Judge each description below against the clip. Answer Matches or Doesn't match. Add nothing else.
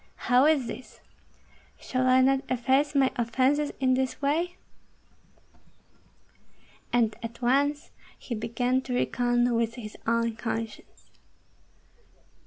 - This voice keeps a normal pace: Doesn't match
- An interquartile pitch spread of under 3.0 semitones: Matches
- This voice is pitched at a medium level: Doesn't match